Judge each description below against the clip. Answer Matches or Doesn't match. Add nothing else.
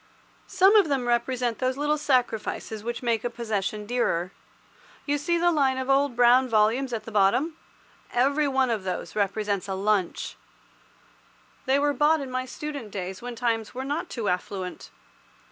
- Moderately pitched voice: Doesn't match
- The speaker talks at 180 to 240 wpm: Doesn't match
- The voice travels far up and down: Doesn't match